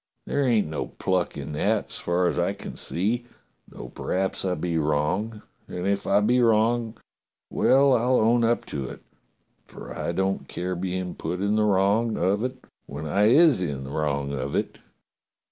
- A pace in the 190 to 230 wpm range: No, average, 180 wpm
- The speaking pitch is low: Yes, very low, 95 Hz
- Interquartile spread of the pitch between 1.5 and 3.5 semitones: No, average, 5.0 semitones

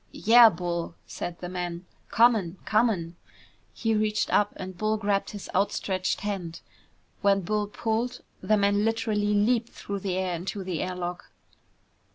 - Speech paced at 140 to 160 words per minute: Yes, average, 150 wpm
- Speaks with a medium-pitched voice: No, high, 200 Hz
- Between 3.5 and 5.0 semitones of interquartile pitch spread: No, average, 3.0 semitones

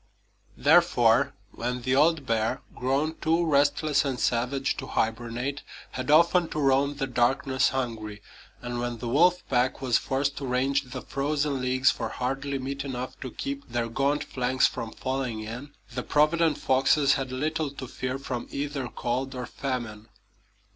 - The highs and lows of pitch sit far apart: No, narrow, 2.4 semitones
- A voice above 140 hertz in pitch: No, low, 135 Hz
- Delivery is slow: No, average, 160 wpm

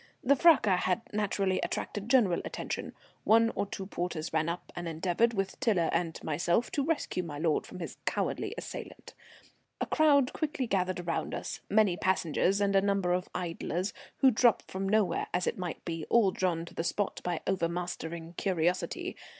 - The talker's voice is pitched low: No, medium, 185 Hz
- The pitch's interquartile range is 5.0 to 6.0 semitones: No, average, 3.7 semitones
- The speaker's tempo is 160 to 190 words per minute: Yes, average, 175 wpm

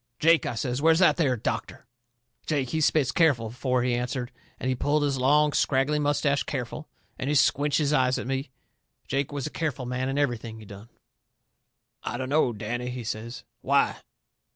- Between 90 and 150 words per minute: No, average, 180 wpm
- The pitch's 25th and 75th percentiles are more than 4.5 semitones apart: No, average, 3.1 semitones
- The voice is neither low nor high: No, low, 130 Hz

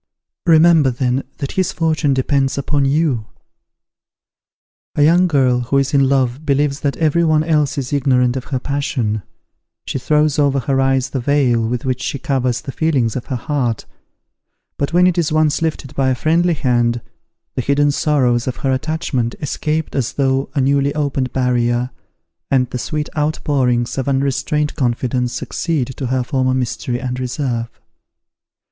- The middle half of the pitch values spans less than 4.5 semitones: Yes, average, 2.9 semitones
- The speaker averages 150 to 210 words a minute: Yes, average, 165 wpm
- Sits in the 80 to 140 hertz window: Yes, low, 135 Hz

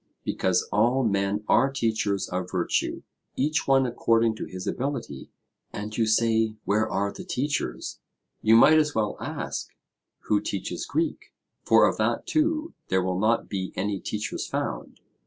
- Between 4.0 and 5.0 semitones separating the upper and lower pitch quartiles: Yes, average, 4.5 semitones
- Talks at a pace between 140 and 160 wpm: Yes, average, 155 wpm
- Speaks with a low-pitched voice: Yes, low, 110 Hz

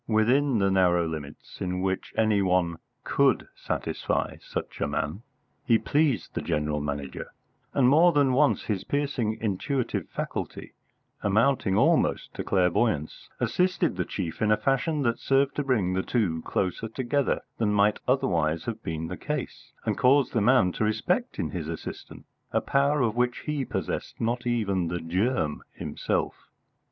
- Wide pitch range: Yes, wide, 6.4 semitones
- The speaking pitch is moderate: No, low, 110 Hz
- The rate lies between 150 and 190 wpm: Yes, average, 160 wpm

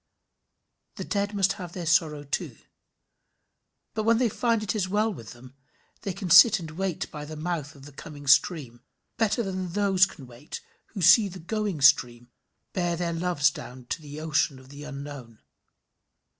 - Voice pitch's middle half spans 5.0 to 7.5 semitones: Yes, average, 5.3 semitones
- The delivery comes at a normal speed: Yes, average, 175 wpm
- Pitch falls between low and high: Yes, medium, 165 Hz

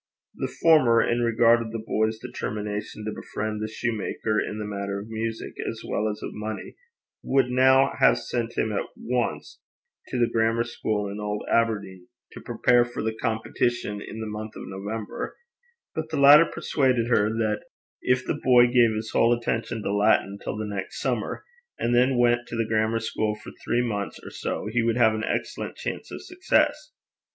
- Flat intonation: Yes, narrow, 2.2 semitones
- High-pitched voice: No, low, 115 Hz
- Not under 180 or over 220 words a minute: Yes, average, 185 wpm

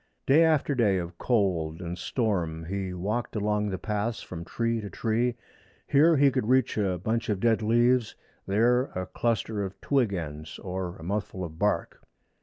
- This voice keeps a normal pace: Yes, average, 175 wpm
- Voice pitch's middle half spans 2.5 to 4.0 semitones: No, average, 4.5 semitones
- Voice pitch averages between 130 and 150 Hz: No, low, 105 Hz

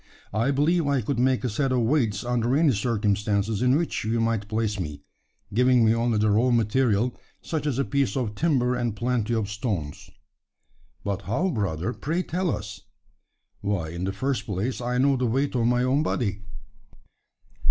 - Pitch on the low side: Yes, low, 120 Hz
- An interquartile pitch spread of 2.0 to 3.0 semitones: No, average, 4.0 semitones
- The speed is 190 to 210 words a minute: No, average, 180 wpm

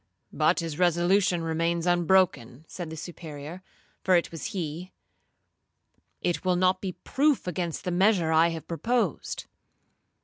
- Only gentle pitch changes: Yes, narrow, 2.3 semitones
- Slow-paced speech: Yes, slow, 130 wpm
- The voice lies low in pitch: No, medium, 175 Hz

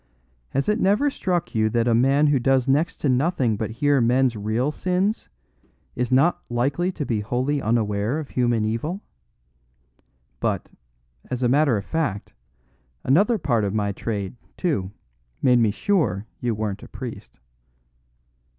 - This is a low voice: Yes, low, 125 Hz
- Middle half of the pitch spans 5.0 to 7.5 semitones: Yes, wide, 5.4 semitones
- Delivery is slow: No, average, 150 wpm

